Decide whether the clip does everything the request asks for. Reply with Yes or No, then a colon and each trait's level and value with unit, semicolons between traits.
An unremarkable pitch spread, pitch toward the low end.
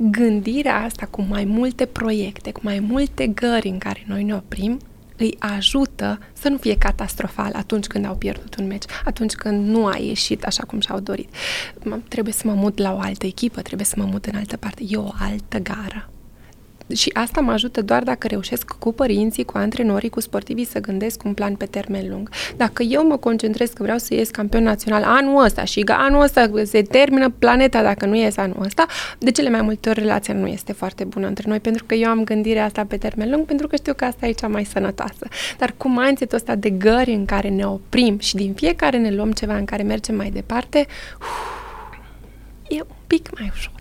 No: average, 3.3 semitones; high, 220 Hz